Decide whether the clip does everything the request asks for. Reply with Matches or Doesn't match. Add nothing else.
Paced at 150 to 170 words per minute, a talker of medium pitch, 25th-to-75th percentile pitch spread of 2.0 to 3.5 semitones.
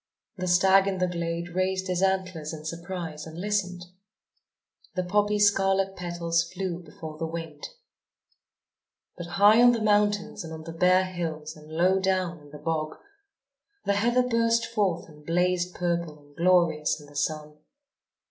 Matches